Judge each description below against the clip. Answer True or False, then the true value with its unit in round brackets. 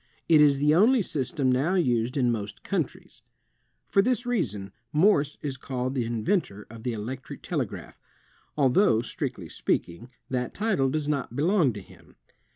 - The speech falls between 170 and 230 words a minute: False (160 wpm)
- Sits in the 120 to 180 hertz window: True (135 Hz)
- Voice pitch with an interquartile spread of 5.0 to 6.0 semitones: True (5.4 semitones)